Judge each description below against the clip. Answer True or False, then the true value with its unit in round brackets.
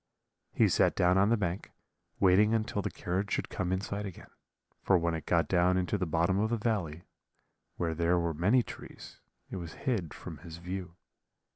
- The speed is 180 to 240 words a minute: True (190 wpm)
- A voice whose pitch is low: True (90 Hz)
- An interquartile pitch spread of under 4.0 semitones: True (3.0 semitones)